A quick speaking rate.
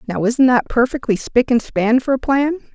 Yes: fast, 220 wpm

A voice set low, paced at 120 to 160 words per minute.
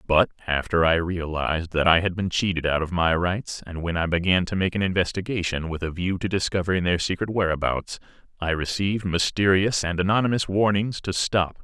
No: very low, 90 Hz; average, 190 wpm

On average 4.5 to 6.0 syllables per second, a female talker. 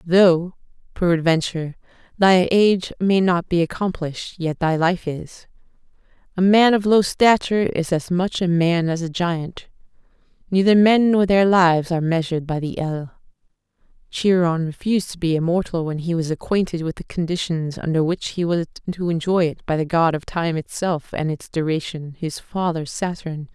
Yes: 4.9 syllables/s; female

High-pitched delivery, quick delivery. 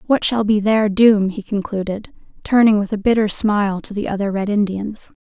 No: high, 205 Hz; average, 195 wpm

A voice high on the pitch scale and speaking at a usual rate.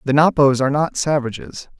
No: medium, 140 Hz; average, 165 wpm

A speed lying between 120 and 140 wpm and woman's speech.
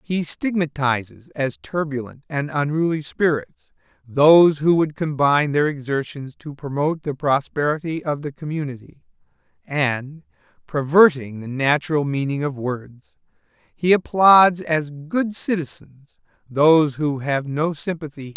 No: slow, 135 wpm; male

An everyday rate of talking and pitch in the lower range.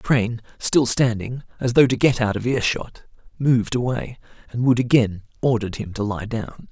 Yes: average, 190 wpm; low, 120 Hz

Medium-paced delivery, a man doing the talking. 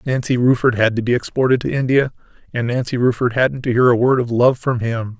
No: fast, 230 wpm; male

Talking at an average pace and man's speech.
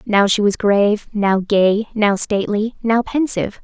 No: average, 165 wpm; female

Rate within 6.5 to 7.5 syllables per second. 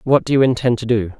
Yes: 6.6 syllables/s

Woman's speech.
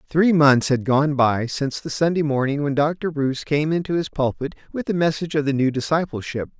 No: male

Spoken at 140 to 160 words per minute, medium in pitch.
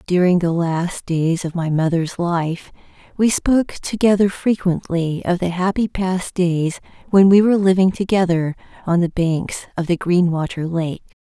Yes: average, 155 wpm; medium, 180 Hz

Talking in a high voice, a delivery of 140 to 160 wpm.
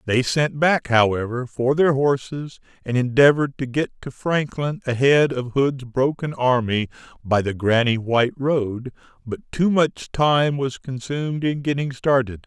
No: low, 130 Hz; average, 155 wpm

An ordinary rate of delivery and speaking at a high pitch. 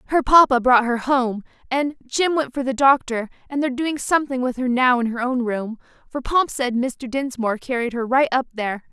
No: fast, 210 wpm; very high, 255 Hz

